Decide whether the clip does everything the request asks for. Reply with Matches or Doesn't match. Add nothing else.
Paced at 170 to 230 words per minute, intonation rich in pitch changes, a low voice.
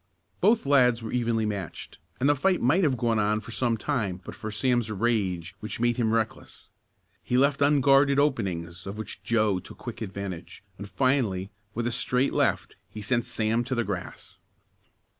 Doesn't match